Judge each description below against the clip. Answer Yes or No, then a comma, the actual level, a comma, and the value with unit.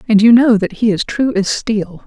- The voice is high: Yes, high, 215 Hz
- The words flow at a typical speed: No, fast, 260 wpm